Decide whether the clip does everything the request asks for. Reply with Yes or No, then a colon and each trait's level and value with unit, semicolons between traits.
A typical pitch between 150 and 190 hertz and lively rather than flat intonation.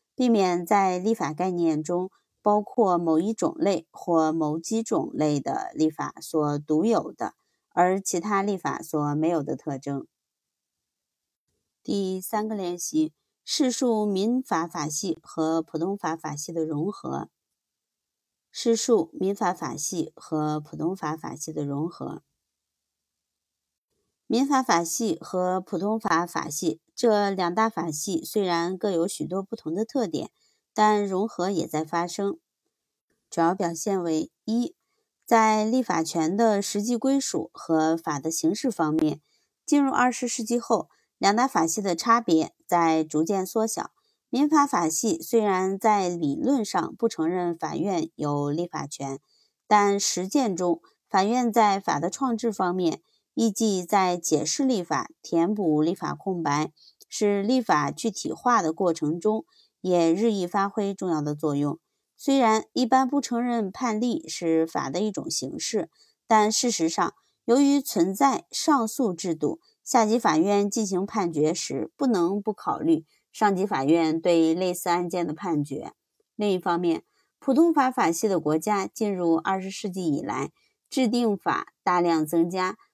Yes: medium, 185 Hz; wide, 5.7 semitones